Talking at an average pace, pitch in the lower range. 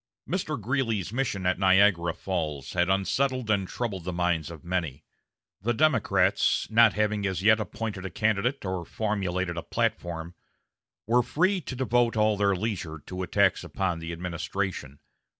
Yes: average, 150 wpm; very low, 95 Hz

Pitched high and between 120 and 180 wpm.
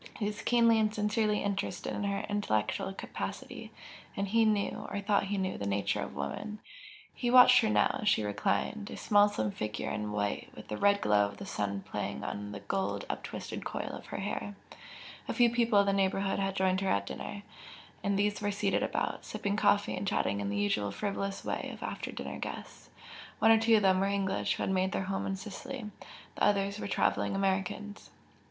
No: high, 200 Hz; fast, 205 wpm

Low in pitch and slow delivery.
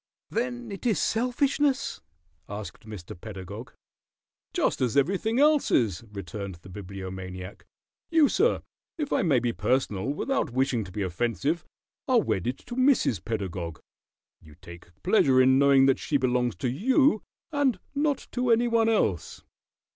No: low, 130 Hz; average, 145 wpm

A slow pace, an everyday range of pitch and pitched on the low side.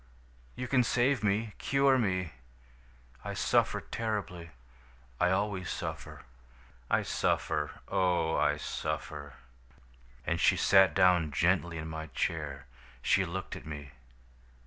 Yes: slow, 120 wpm; average, 4.7 semitones; very low, 90 Hz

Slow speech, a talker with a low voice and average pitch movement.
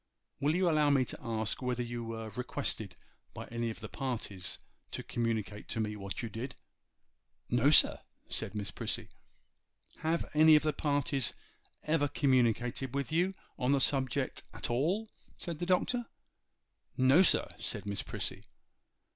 No: average, 155 wpm; low, 130 Hz; average, 4.9 semitones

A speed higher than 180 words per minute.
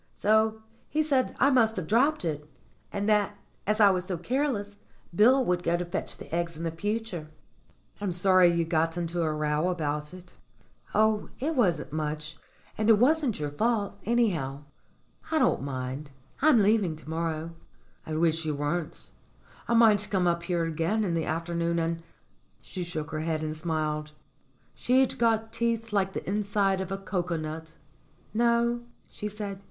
No: average, 170 wpm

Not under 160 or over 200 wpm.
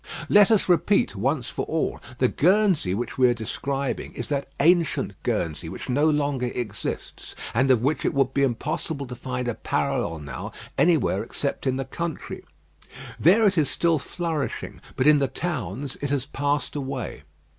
Yes: average, 170 wpm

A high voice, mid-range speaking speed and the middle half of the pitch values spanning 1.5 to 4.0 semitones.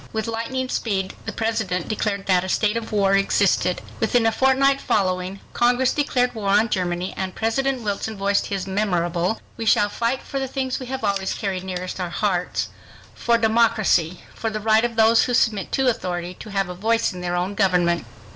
Yes: high, 210 Hz; average, 185 wpm; average, 3.7 semitones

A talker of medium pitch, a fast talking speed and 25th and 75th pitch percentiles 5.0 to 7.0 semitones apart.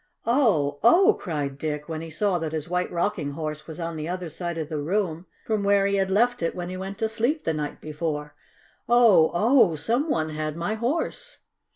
Yes: medium, 175 Hz; fast, 210 wpm; wide, 5.5 semitones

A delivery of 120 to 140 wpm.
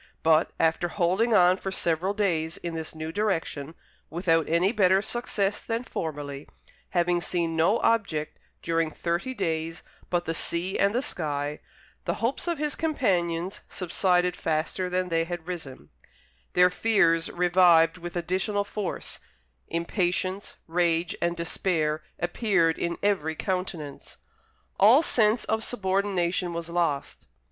Yes: slow, 135 wpm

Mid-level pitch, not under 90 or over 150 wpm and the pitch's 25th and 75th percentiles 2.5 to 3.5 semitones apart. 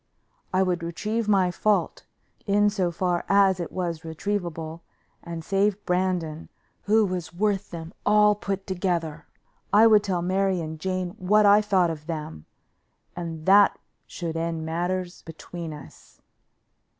Yes: medium, 180 Hz; average, 140 wpm; average, 3.2 semitones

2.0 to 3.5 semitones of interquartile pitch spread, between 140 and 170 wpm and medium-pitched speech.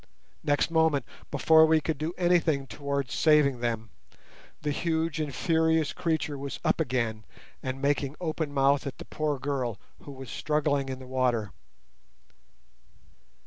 Yes: average, 3.2 semitones; average, 145 wpm; medium, 145 Hz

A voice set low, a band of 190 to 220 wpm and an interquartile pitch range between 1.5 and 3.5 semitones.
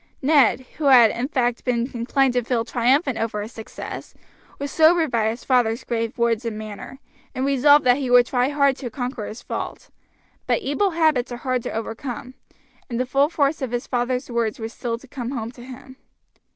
No: very high, 250 Hz; average, 200 wpm; average, 2.8 semitones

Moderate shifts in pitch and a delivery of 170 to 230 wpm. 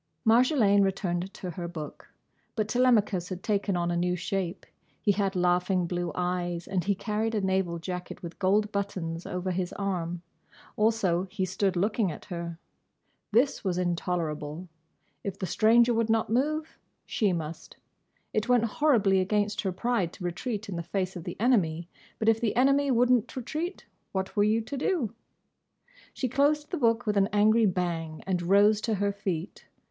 Yes: average, 4.0 semitones; average, 175 wpm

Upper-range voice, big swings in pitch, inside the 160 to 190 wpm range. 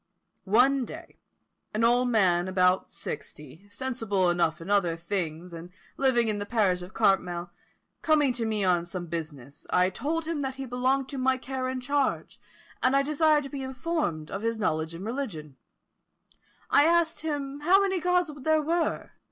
Yes: high, 235 Hz; wide, 7.6 semitones; average, 170 wpm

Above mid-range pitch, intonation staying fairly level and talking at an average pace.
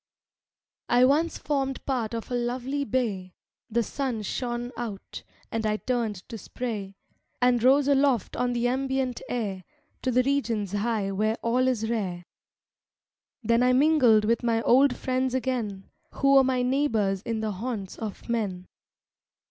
No: high, 240 Hz; average, 3.2 semitones; average, 150 wpm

